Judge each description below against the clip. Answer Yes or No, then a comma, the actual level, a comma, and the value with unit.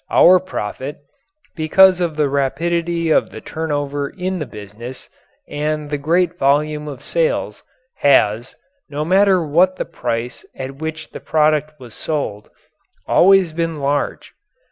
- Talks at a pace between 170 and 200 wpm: No, slow, 135 wpm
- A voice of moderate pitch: Yes, medium, 150 Hz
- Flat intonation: No, average, 3.6 semitones